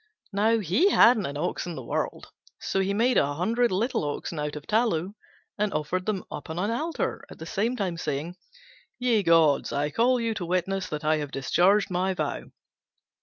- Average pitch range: No, wide, 6.0 semitones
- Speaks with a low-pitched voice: No, medium, 185 Hz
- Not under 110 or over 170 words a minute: No, average, 195 wpm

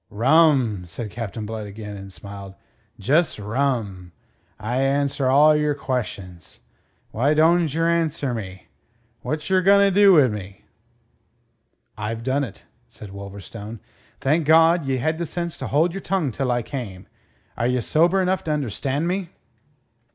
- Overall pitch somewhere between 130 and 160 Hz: Yes, low, 135 Hz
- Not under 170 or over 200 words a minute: No, average, 140 wpm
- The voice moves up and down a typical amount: No, wide, 7.1 semitones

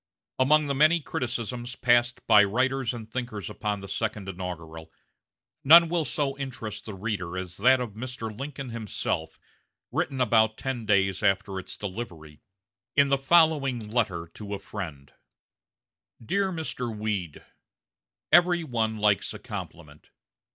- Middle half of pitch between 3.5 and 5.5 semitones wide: Yes, average, 5.1 semitones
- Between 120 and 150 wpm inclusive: Yes, slow, 135 wpm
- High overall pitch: No, low, 110 Hz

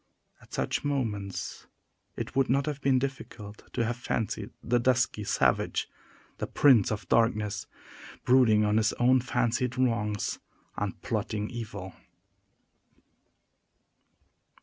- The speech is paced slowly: Yes, slow, 115 wpm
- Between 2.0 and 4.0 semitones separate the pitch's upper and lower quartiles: Yes, average, 3.4 semitones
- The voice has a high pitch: No, low, 115 Hz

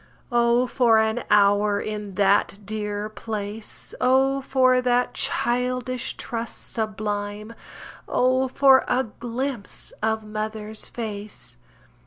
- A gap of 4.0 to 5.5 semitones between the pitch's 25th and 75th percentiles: No, average, 3.0 semitones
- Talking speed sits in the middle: No, slow, 105 wpm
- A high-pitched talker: Yes, high, 220 Hz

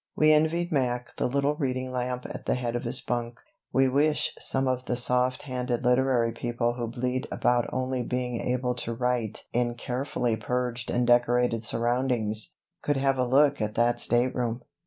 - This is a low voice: Yes, low, 125 Hz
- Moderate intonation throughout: No, narrow, 1.3 semitones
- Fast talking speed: No, average, 175 wpm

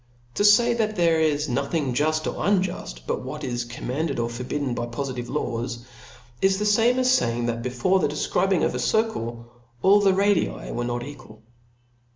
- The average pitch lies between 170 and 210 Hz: No, medium, 145 Hz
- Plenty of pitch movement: Yes, wide, 8.1 semitones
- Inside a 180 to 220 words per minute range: Yes, average, 190 wpm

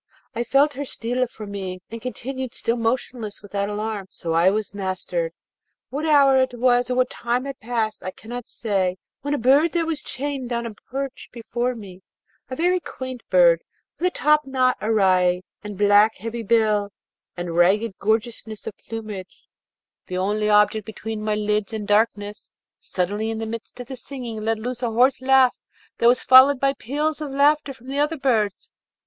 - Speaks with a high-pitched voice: Yes, high, 230 Hz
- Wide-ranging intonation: No, average, 3.9 semitones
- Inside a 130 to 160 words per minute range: No, average, 180 wpm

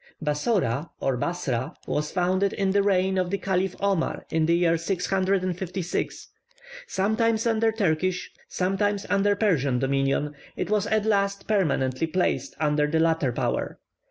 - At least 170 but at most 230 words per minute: No, average, 140 wpm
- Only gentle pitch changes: No, average, 4.2 semitones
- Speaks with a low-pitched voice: No, medium, 185 Hz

